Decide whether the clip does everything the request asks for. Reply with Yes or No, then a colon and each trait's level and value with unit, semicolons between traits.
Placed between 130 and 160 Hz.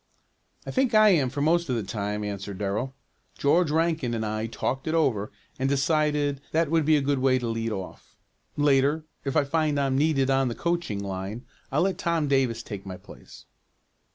Yes: low, 135 Hz